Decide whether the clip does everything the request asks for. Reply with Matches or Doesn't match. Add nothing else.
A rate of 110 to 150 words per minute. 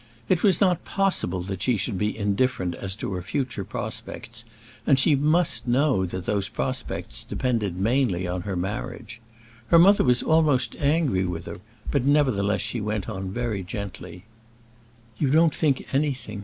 Doesn't match